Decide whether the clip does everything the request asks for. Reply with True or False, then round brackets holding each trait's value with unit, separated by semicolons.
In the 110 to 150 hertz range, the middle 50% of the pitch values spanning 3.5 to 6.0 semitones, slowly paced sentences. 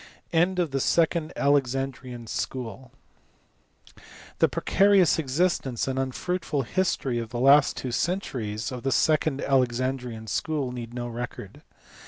True (135 Hz; 4.2 semitones; 125 wpm)